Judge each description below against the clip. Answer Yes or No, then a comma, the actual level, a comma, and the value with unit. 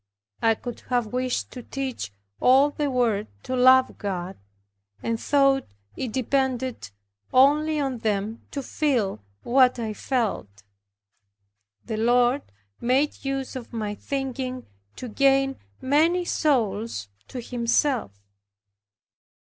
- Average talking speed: No, slow, 115 wpm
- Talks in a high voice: Yes, very high, 255 Hz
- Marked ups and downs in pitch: No, average, 3.2 semitones